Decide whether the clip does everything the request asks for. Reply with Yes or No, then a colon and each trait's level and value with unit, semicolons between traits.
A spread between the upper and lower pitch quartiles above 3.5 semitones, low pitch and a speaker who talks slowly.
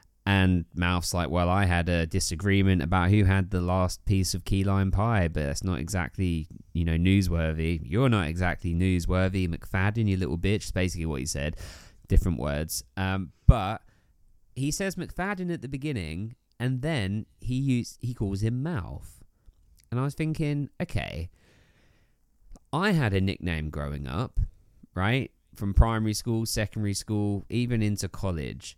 No: average, 4.2 semitones; very low, 95 Hz; average, 155 wpm